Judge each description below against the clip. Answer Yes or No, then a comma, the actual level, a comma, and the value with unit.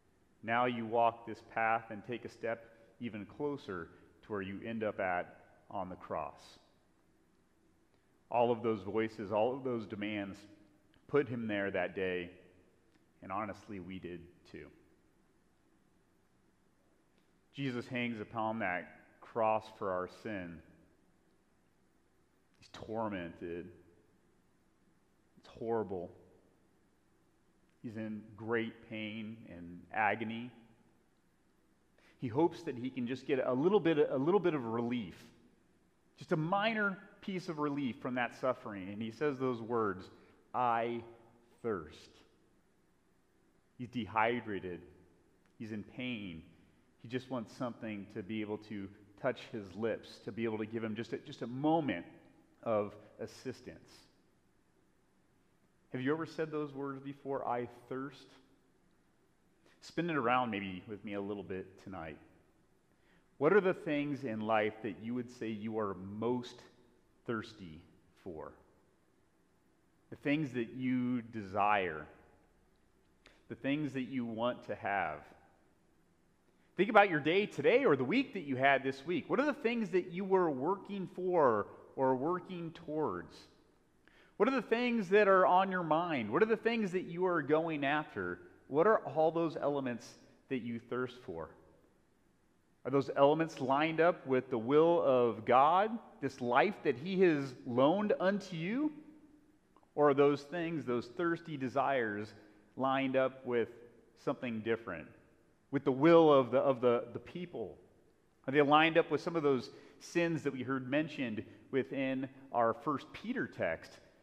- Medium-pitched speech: No, low, 125 Hz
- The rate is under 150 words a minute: Yes, average, 140 wpm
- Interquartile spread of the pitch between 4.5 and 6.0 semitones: Yes, wide, 5.6 semitones